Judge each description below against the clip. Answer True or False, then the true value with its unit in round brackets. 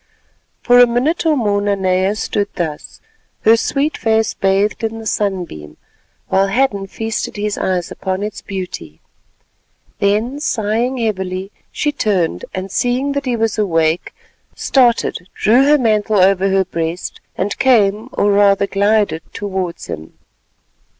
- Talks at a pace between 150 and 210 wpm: False (135 wpm)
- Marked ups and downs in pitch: False (3.3 semitones)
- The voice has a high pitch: True (205 Hz)